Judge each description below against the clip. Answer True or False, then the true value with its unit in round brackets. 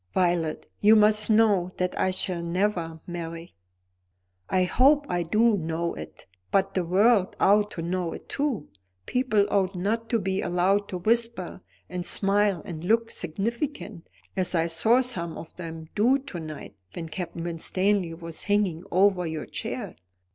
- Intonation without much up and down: False (3.7 semitones)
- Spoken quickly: False (155 wpm)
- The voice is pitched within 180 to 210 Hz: True (185 Hz)